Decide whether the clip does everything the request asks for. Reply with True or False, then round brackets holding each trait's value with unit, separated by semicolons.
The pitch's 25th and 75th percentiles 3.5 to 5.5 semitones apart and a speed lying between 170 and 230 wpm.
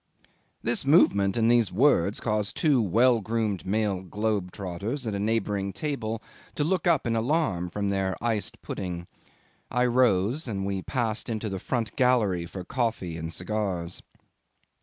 False (3.8 semitones; 155 wpm)